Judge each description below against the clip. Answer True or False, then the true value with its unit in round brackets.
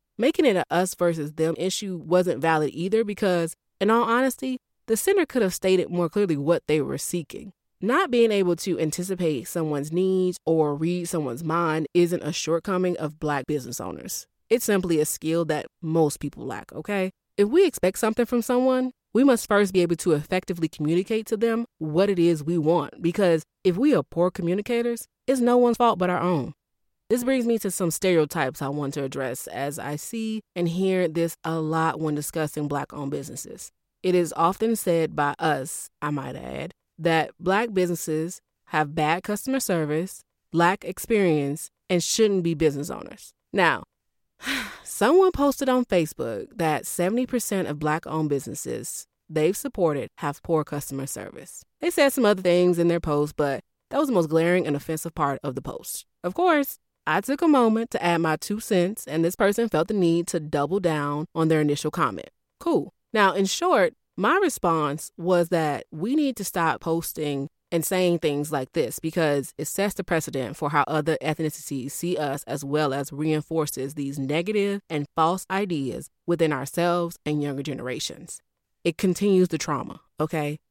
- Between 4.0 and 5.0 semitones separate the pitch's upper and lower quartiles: True (4.4 semitones)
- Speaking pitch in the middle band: True (170 Hz)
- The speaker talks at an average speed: True (180 wpm)